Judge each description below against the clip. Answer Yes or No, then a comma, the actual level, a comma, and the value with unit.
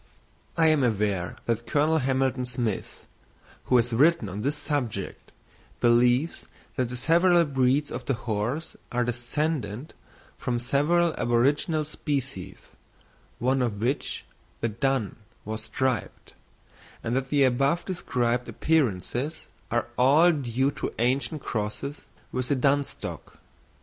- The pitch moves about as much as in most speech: Yes, average, 3.6 semitones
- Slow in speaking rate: Yes, slow, 125 wpm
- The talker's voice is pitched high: No, low, 130 Hz